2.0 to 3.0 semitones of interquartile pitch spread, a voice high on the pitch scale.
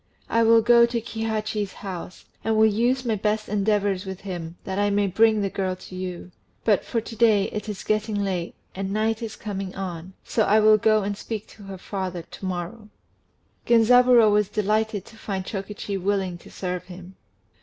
Yes: narrow, 2.5 semitones; high, 205 Hz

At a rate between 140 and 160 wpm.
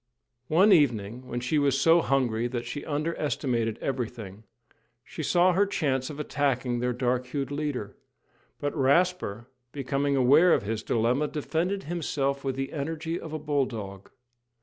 Yes: average, 150 wpm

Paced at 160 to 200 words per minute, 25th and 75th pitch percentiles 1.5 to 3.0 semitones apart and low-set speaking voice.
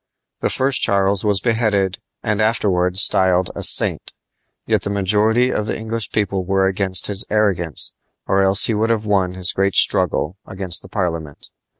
Yes: average, 165 wpm; narrow, 2.4 semitones; low, 100 Hz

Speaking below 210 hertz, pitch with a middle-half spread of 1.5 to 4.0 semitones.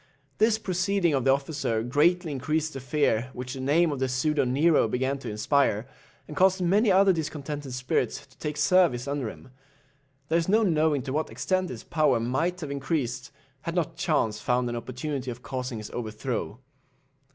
No: medium, 140 Hz; average, 4.7 semitones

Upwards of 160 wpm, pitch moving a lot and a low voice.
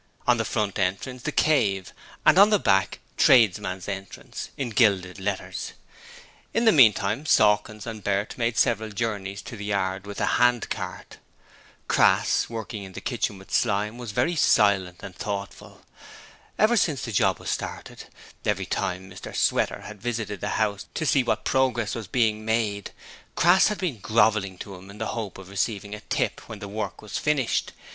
No: average, 175 wpm; average, 3.4 semitones; low, 105 Hz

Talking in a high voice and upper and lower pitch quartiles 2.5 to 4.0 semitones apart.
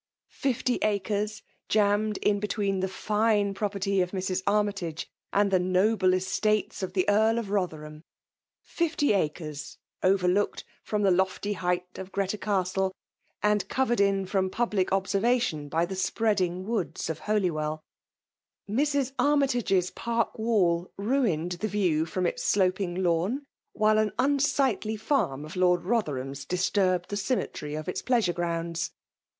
Yes: high, 195 Hz; average, 3.1 semitones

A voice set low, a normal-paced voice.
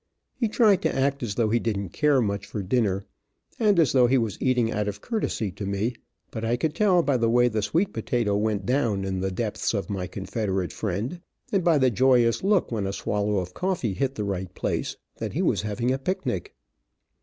No: low, 115 Hz; fast, 215 wpm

